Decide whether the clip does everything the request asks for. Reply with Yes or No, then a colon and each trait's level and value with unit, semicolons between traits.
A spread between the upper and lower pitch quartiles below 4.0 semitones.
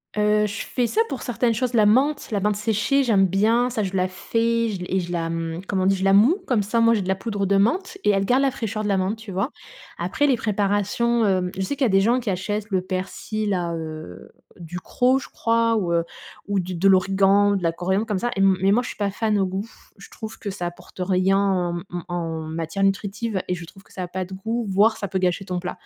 Yes: average, 3.3 semitones